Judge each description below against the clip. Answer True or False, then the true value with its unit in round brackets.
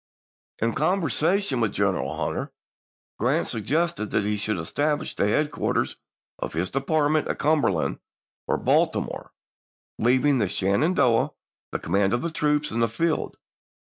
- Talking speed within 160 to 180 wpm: False (140 wpm)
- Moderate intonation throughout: False (6.8 semitones)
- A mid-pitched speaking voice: False (130 Hz)